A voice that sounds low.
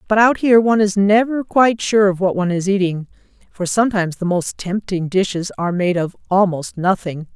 No: high, 195 Hz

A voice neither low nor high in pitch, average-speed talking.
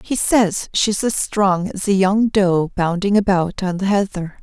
No: high, 195 Hz; average, 190 wpm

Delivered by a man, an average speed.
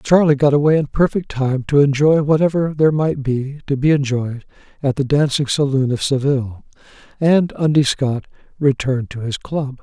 Yes: male; average, 170 wpm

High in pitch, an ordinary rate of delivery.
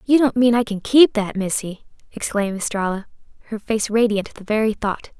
Yes: high, 215 Hz; average, 195 wpm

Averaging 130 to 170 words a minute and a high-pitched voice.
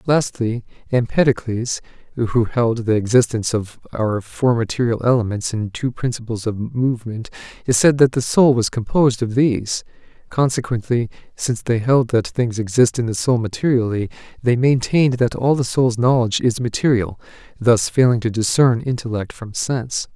No: average, 150 wpm; low, 120 Hz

